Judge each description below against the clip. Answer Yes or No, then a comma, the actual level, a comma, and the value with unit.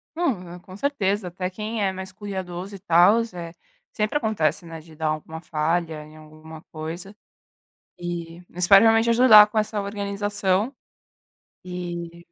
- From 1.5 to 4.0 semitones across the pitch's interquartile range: Yes, average, 3.7 semitones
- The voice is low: No, medium, 185 Hz